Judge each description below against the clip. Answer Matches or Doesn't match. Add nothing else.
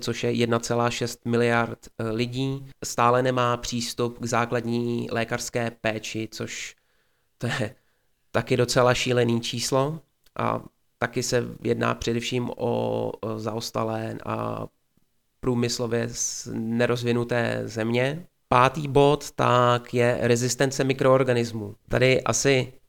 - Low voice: Matches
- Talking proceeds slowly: Matches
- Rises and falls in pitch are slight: Matches